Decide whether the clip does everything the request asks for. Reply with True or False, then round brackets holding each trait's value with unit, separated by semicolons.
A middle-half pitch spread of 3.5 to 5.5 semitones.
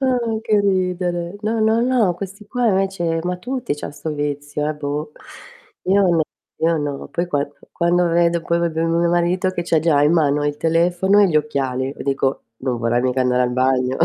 True (4.3 semitones)